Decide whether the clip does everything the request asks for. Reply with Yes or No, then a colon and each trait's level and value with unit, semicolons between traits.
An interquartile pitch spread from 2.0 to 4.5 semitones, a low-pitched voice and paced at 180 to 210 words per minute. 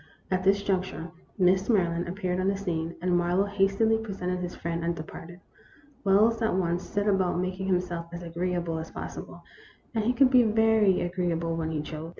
No: narrow, 2.6 semitones; medium, 180 Hz; average, 190 wpm